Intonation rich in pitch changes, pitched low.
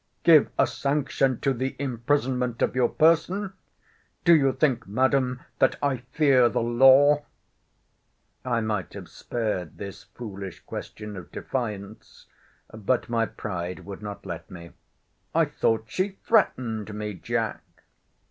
No: average, 4.5 semitones; low, 120 Hz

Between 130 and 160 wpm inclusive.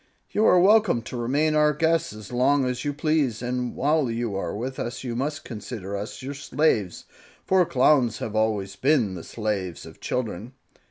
No: average, 180 wpm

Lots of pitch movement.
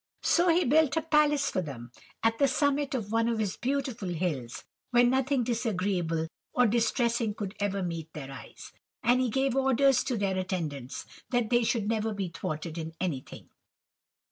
Yes: wide, 6.5 semitones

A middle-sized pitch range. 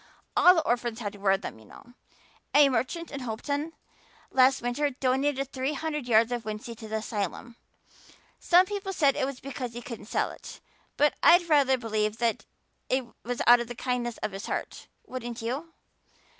Yes: average, 3.7 semitones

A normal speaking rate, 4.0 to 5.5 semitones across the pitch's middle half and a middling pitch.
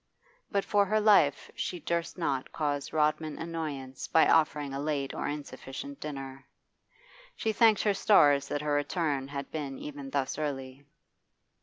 No: average, 150 wpm; average, 3.1 semitones; medium, 145 Hz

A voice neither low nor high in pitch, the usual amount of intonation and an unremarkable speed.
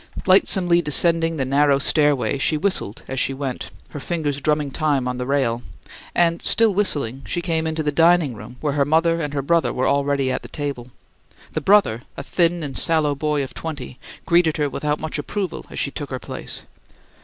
Yes: medium, 150 Hz; average, 3.3 semitones; average, 195 wpm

